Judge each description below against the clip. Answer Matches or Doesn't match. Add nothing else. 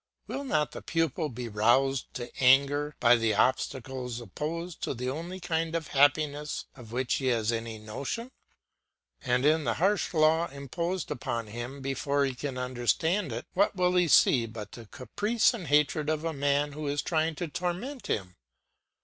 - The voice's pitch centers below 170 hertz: Matches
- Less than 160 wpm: Doesn't match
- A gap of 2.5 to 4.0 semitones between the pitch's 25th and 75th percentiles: Doesn't match